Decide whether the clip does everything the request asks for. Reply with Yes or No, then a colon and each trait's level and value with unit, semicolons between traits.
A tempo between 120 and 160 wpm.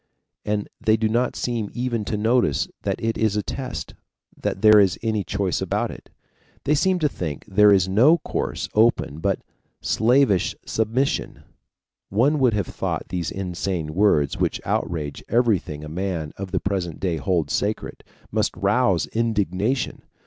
Yes: average, 155 wpm